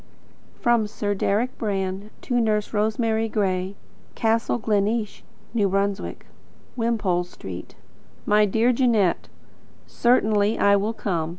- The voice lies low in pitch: No, high, 210 Hz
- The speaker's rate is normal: No, slow, 110 wpm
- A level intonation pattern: Yes, narrow, 2.3 semitones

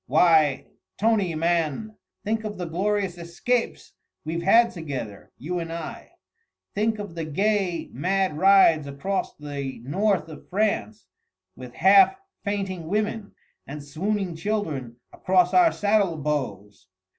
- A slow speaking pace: Yes, slow, 125 wpm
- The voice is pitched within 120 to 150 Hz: No, medium, 180 Hz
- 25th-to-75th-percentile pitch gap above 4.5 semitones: Yes, average, 4.9 semitones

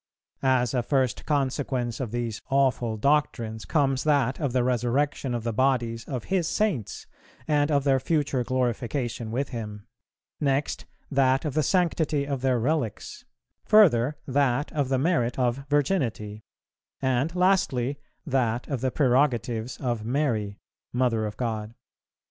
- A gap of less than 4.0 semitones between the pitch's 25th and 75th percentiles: Yes, average, 3.3 semitones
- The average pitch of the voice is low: Yes, low, 130 Hz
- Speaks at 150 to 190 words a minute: No, average, 140 wpm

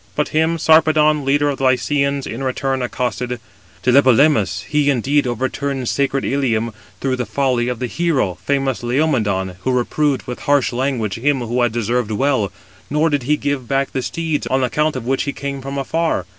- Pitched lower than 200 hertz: Yes, low, 135 Hz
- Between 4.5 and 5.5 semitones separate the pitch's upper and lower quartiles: No, average, 2.9 semitones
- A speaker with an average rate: Yes, average, 180 wpm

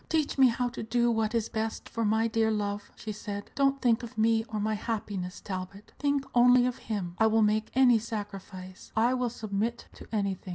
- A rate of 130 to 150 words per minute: No, fast, 205 wpm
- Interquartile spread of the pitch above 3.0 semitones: No, narrow, 2.5 semitones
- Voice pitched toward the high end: Yes, high, 220 Hz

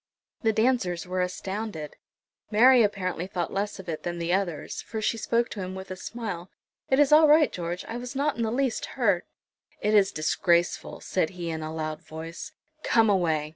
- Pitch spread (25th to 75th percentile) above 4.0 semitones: Yes, average, 5.0 semitones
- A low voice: No, high, 190 Hz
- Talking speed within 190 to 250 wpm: Yes, average, 195 wpm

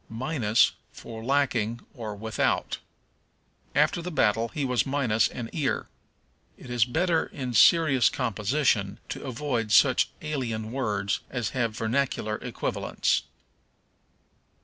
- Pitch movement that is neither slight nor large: Yes, average, 4.0 semitones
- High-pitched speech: No, low, 120 Hz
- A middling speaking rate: No, slow, 115 wpm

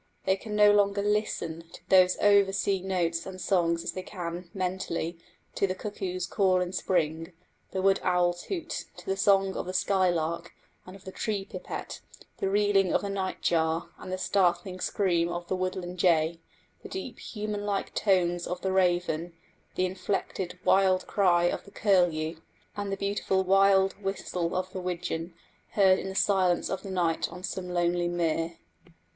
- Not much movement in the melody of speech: Yes, narrow, 1.9 semitones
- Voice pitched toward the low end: No, medium, 185 Hz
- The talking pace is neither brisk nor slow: Yes, average, 175 wpm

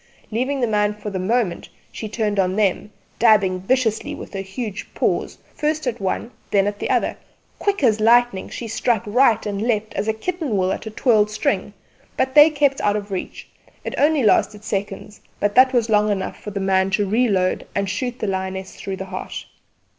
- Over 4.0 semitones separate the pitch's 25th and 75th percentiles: No, average, 3.6 semitones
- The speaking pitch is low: No, high, 210 Hz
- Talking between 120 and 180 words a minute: No, average, 200 wpm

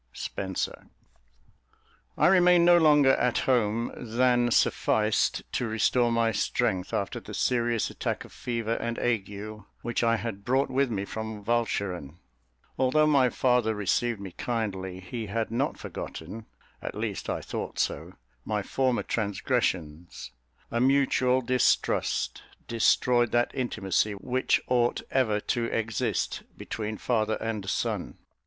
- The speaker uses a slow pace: Yes, slow, 130 wpm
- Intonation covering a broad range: No, average, 3.0 semitones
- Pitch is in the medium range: No, low, 115 Hz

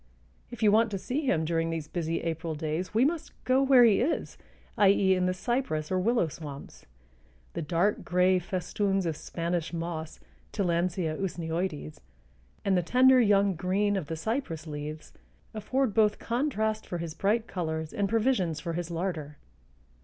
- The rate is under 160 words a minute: No, average, 165 wpm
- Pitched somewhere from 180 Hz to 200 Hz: Yes, medium, 185 Hz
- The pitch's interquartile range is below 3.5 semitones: No, average, 4.7 semitones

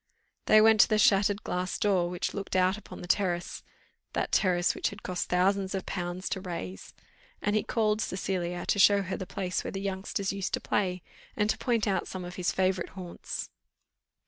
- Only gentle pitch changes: Yes, narrow, 2.1 semitones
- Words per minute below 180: No, average, 200 wpm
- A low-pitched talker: No, high, 190 Hz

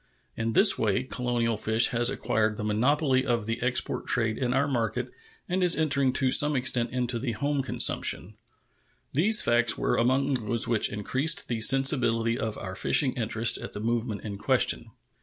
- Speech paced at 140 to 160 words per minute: No, average, 175 wpm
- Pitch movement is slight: No, average, 3.1 semitones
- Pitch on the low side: Yes, low, 120 Hz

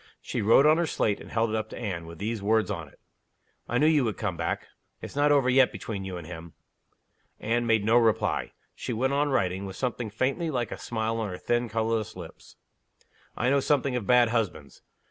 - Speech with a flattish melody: No, average, 3.9 semitones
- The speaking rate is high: Yes, fast, 220 wpm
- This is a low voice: Yes, low, 115 Hz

